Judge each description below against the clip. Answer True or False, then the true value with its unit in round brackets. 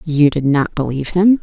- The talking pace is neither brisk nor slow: False (210 wpm)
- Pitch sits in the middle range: True (155 Hz)